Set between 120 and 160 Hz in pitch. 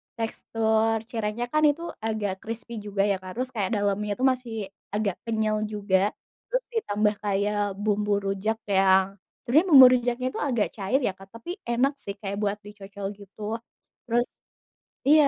No: high, 215 Hz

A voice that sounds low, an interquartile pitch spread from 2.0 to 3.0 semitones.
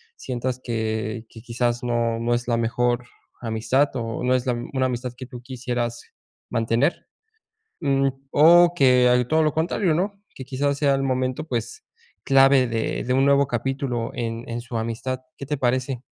Yes: low, 125 Hz; narrow, 2.4 semitones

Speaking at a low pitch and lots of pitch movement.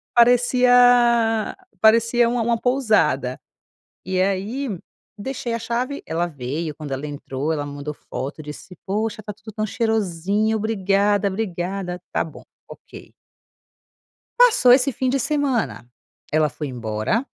No: high, 210 Hz; wide, 6.8 semitones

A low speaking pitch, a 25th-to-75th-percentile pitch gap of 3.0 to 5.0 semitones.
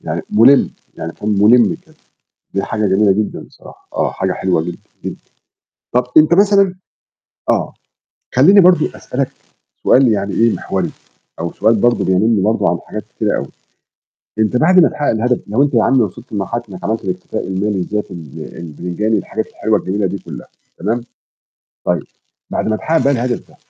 Yes: low, 110 Hz; average, 4.6 semitones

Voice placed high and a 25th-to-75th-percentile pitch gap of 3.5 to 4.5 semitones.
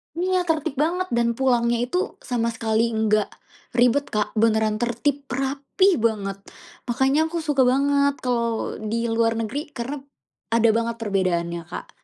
Yes: high, 240 Hz; average, 4.1 semitones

